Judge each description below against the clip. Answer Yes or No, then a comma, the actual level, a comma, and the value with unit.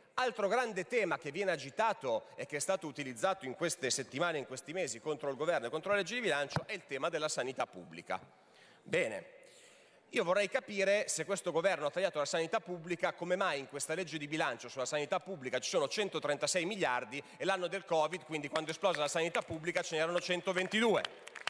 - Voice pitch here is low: No, medium, 170 Hz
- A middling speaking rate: No, fast, 200 wpm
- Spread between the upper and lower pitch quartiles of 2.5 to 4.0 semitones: No, average, 4.5 semitones